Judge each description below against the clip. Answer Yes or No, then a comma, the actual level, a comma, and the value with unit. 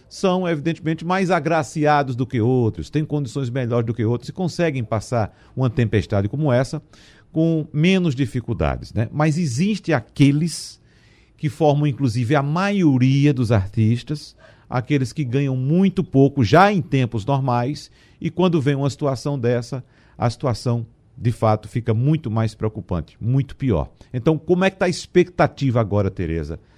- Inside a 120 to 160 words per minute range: Yes, average, 150 wpm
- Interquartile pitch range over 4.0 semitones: Yes, average, 4.9 semitones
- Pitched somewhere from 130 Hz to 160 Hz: Yes, low, 135 Hz